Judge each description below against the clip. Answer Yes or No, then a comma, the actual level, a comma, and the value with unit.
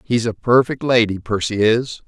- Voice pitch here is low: Yes, low, 115 Hz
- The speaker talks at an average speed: Yes, average, 175 wpm